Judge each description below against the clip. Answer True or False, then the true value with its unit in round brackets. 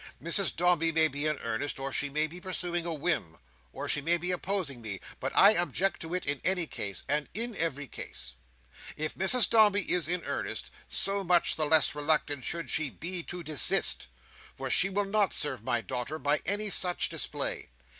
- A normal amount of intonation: True (4.0 semitones)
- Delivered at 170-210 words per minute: True (195 wpm)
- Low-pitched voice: False (165 Hz)